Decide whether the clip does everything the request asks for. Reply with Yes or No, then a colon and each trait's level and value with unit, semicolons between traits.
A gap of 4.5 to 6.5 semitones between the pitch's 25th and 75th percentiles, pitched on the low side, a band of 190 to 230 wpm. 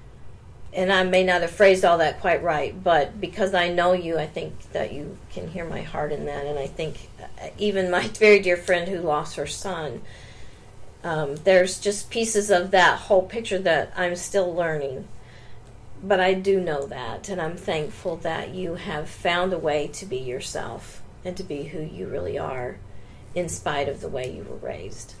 No: average, 5.2 semitones; medium, 175 Hz; average, 195 wpm